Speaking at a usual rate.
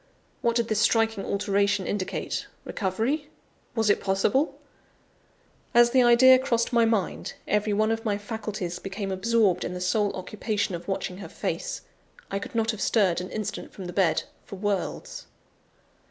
Yes: average, 160 wpm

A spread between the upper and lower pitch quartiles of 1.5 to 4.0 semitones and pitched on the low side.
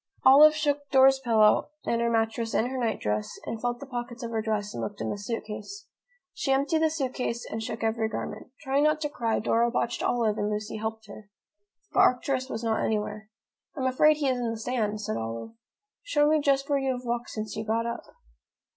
No: average, 3.5 semitones; high, 235 Hz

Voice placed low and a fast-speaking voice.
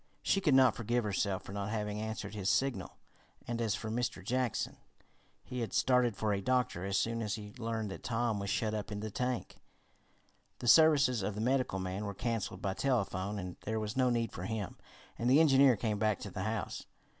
Yes: low, 110 Hz; fast, 210 wpm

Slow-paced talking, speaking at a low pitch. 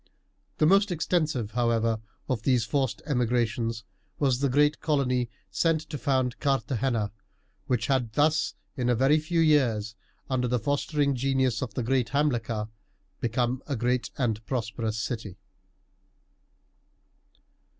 Yes: slow, 130 wpm; low, 125 Hz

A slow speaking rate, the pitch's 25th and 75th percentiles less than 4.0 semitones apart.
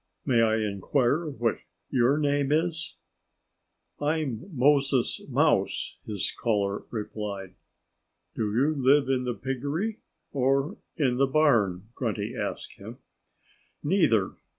No: slow, 110 wpm; average, 4.5 semitones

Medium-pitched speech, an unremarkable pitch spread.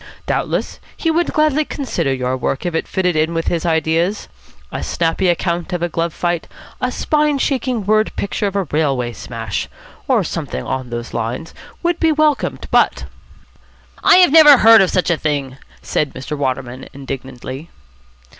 No: medium, 170 Hz; wide, 8.8 semitones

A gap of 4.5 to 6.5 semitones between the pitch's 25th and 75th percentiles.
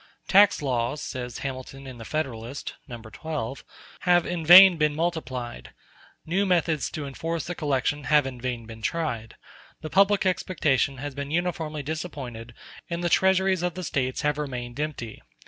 Yes: average, 5.1 semitones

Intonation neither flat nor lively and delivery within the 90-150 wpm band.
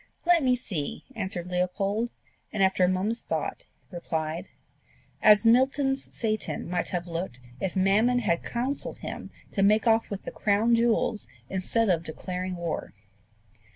Yes: average, 4.4 semitones; average, 145 wpm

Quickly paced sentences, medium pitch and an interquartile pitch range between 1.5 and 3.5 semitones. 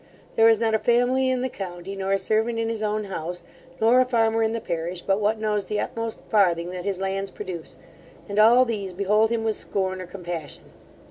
No: fast, 215 wpm; high, 210 Hz; average, 3.0 semitones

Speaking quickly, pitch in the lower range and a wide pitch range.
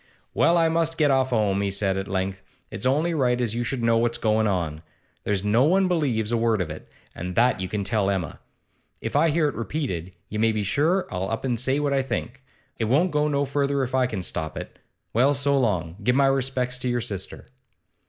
Yes: fast, 230 wpm; low, 120 Hz; wide, 5.7 semitones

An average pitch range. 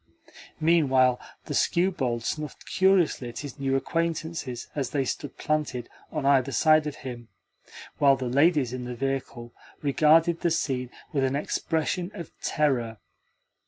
Yes: average, 3.8 semitones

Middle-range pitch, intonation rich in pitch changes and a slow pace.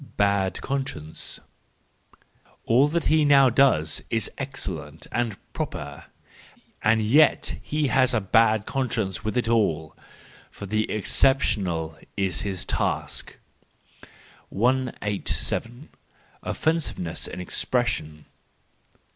No: low, 110 Hz; wide, 5.8 semitones; slow, 100 wpm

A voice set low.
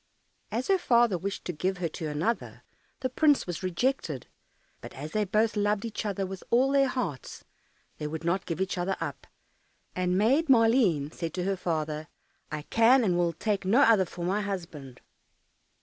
No: high, 195 Hz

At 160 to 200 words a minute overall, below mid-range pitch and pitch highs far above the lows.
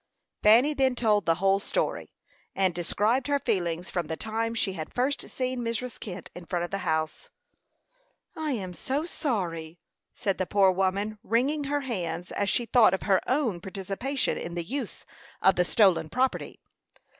No: average, 170 wpm; high, 200 Hz; wide, 5.8 semitones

